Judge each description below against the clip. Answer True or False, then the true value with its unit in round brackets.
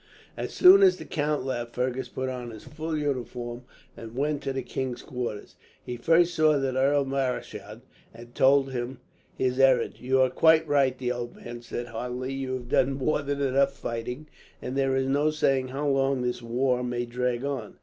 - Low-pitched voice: True (130 Hz)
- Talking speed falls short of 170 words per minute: False (190 wpm)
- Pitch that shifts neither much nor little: False (2.1 semitones)